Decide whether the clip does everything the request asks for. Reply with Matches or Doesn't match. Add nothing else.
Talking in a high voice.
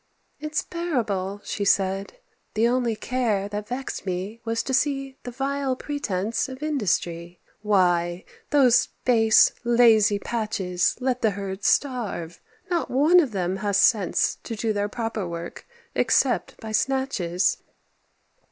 Matches